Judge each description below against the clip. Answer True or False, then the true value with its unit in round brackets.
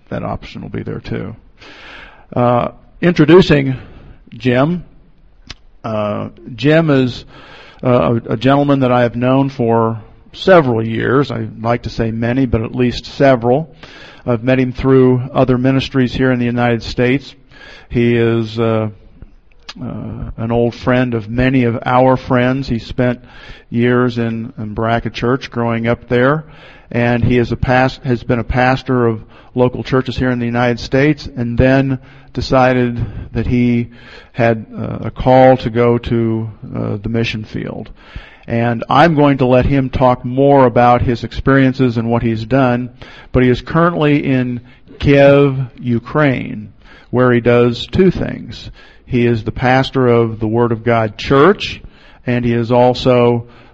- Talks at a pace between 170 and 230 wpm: False (155 wpm)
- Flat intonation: True (2.0 semitones)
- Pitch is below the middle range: True (125 Hz)